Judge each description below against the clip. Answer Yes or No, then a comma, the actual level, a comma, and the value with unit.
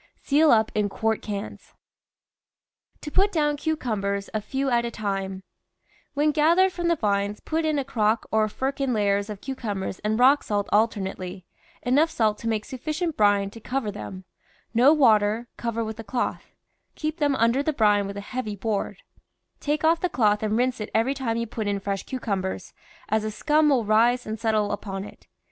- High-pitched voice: Yes, high, 225 Hz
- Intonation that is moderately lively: Yes, average, 5.0 semitones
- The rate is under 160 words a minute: No, average, 190 wpm